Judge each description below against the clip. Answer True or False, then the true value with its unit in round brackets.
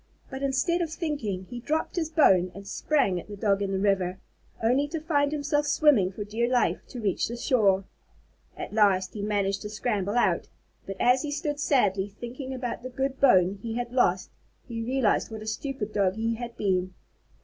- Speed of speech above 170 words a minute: True (195 wpm)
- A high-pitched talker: True (230 Hz)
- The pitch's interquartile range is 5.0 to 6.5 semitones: True (5.4 semitones)